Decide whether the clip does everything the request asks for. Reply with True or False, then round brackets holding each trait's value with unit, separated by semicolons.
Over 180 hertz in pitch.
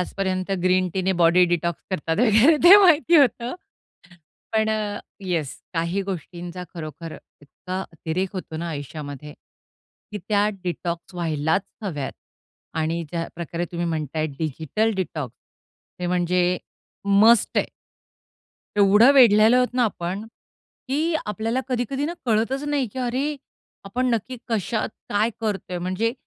True (190 Hz)